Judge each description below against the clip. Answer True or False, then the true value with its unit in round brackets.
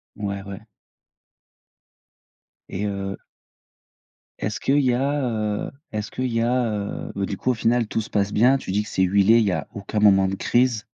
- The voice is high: False (105 Hz)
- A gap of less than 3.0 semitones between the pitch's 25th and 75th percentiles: False (3.4 semitones)